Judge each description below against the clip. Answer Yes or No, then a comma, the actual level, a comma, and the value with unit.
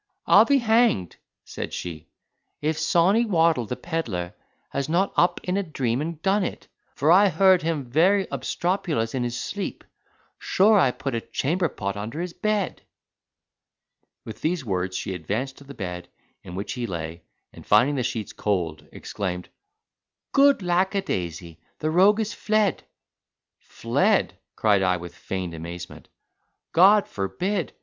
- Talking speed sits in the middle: Yes, average, 145 wpm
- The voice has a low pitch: No, medium, 145 Hz